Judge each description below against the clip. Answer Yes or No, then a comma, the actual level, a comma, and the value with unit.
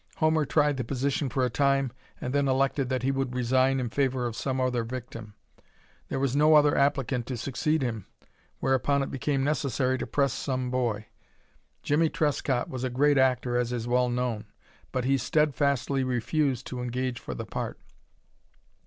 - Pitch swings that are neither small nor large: No, narrow, 2.0 semitones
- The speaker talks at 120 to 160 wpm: No, average, 175 wpm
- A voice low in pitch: Yes, low, 130 Hz